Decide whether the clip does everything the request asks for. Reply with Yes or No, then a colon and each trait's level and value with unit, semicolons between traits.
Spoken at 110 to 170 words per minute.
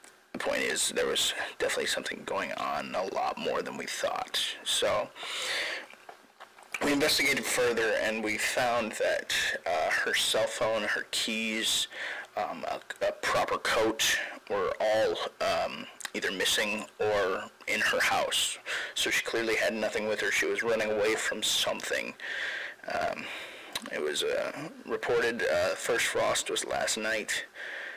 Yes: average, 145 wpm